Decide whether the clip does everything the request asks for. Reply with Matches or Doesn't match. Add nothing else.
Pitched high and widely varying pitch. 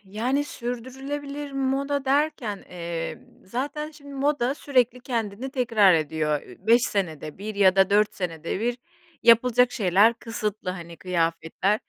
Matches